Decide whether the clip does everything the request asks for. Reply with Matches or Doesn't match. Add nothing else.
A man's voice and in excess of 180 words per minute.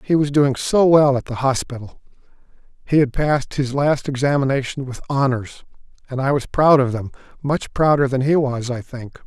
Matches